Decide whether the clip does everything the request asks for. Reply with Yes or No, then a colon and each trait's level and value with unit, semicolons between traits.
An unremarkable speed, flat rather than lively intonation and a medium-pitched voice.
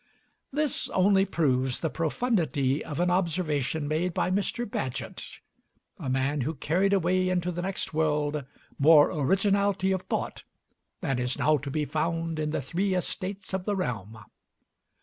No: average, 150 wpm; average, 4.5 semitones; medium, 165 Hz